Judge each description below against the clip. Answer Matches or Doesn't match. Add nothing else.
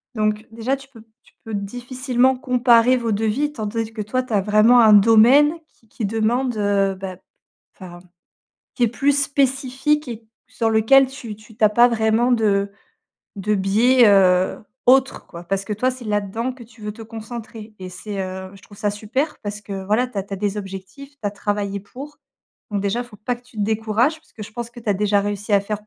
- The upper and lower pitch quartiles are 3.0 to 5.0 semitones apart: Matches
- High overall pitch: Matches